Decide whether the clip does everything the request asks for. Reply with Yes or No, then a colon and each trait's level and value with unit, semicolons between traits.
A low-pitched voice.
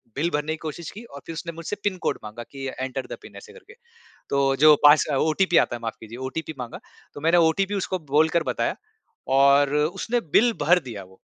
No: medium, 155 Hz